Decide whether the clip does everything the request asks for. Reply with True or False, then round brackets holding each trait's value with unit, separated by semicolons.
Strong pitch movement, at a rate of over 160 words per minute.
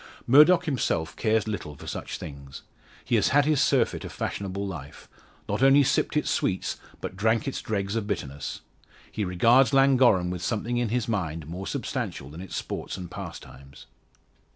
True (6.0 semitones; 170 wpm)